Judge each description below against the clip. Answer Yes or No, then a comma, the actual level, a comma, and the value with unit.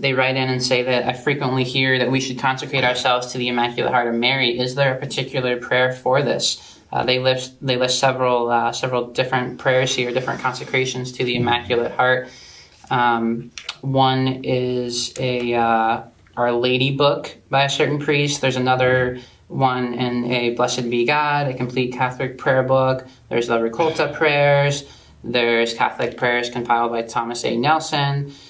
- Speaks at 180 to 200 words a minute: No, average, 170 wpm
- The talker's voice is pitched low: Yes, low, 125 Hz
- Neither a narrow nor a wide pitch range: No, narrow, 1.4 semitones